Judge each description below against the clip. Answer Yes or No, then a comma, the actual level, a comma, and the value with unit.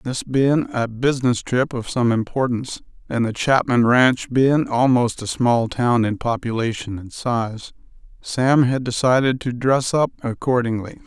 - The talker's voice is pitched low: Yes, low, 125 Hz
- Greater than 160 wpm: No, average, 150 wpm